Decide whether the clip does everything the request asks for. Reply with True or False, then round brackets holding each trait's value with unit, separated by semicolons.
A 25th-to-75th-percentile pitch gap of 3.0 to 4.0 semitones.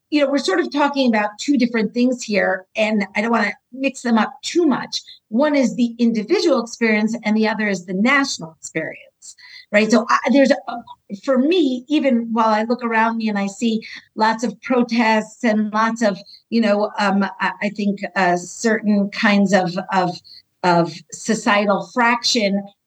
True (3.5 semitones)